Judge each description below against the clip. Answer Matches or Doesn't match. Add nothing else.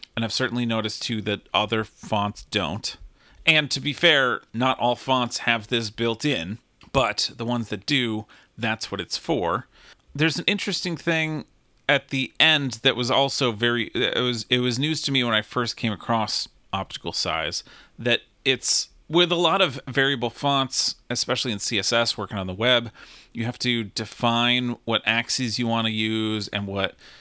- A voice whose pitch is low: Matches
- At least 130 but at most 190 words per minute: Matches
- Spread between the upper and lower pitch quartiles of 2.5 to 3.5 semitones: Matches